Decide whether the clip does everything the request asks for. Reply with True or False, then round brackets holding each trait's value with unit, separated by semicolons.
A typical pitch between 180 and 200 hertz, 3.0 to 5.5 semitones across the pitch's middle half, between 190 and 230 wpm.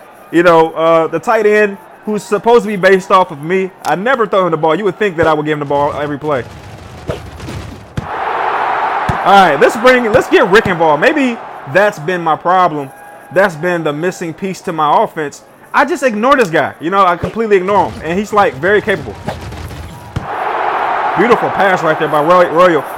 True (185 Hz; 4.8 semitones; 195 wpm)